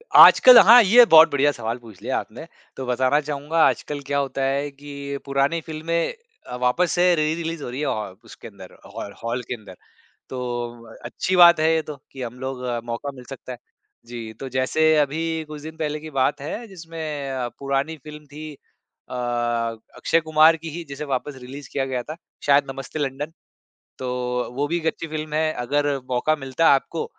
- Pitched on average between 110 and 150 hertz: Yes, medium, 140 Hz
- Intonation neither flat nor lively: Yes, average, 3.8 semitones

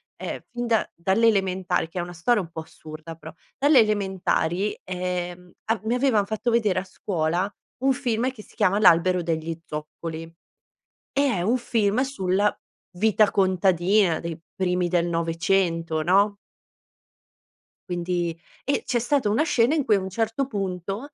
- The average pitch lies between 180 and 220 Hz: Yes, high, 190 Hz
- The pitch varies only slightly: No, average, 4.3 semitones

